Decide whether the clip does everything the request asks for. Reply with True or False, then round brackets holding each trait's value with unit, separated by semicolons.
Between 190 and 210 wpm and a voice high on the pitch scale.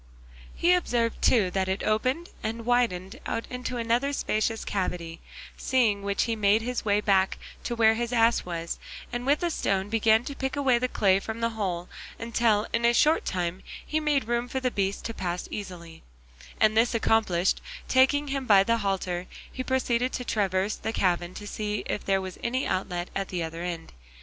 True (195 wpm; 220 Hz)